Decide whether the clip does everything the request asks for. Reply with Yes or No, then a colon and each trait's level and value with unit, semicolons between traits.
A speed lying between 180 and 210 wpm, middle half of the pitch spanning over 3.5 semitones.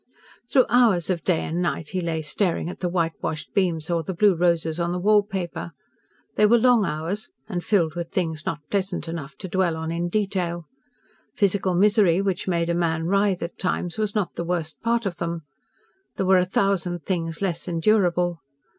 No: average, 190 wpm; average, 2.8 semitones